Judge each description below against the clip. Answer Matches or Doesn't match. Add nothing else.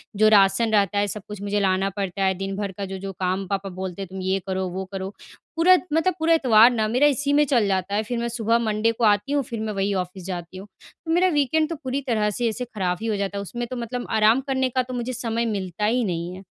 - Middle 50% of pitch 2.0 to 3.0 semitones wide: Doesn't match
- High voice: Matches